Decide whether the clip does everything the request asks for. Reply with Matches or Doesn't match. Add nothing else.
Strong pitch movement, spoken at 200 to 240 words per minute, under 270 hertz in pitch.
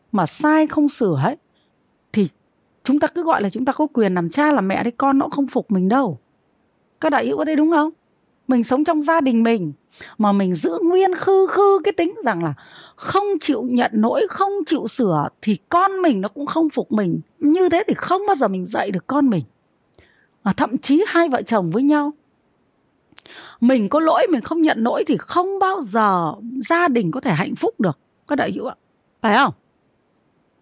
Doesn't match